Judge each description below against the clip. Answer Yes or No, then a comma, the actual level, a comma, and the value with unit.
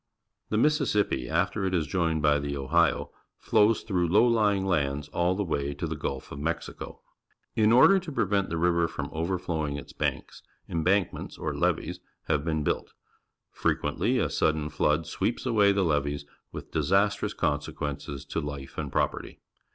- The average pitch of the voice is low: Yes, very low, 85 Hz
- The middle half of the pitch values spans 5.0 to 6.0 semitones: Yes, wide, 5.4 semitones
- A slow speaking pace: No, average, 160 wpm